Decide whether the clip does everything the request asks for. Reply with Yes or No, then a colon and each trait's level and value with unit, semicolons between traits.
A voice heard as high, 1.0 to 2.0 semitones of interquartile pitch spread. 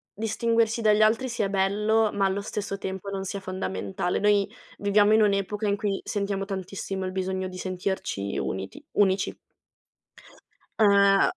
Yes: high, 200 Hz; narrow, 1.7 semitones